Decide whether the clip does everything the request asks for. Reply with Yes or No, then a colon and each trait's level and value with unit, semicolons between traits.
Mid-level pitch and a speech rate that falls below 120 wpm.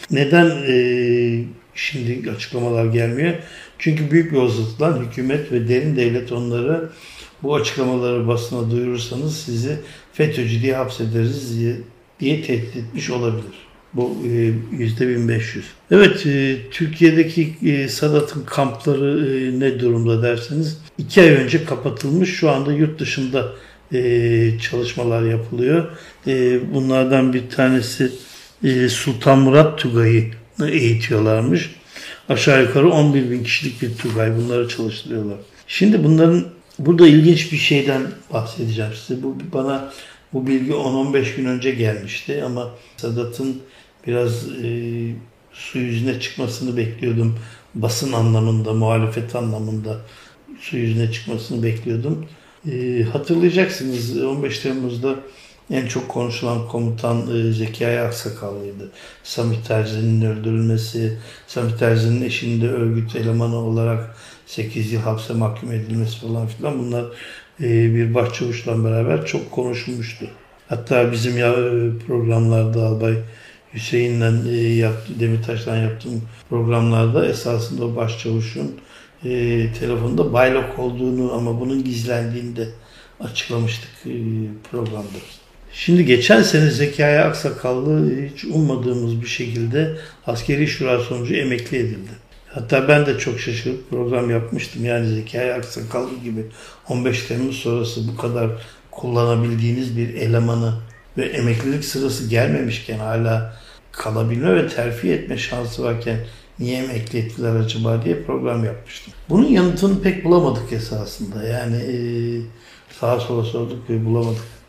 No: low, 120 Hz; average, 110 wpm